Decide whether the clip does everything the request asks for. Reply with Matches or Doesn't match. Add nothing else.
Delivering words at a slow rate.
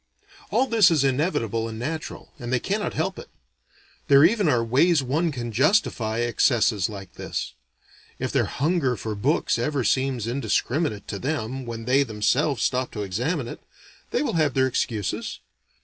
Doesn't match